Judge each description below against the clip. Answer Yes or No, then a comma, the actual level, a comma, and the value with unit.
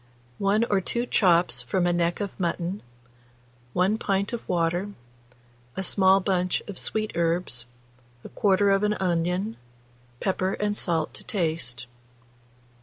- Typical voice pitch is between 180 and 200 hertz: Yes, medium, 185 Hz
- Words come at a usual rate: No, slow, 130 wpm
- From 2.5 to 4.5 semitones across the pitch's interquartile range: Yes, average, 2.9 semitones